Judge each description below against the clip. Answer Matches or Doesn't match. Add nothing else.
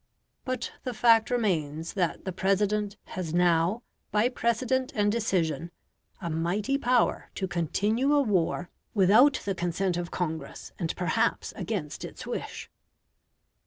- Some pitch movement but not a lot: Matches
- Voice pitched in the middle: Doesn't match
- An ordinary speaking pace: Doesn't match